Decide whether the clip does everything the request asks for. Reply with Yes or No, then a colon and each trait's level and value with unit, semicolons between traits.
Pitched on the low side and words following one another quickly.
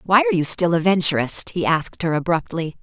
No: medium, 180 Hz; fast, 215 wpm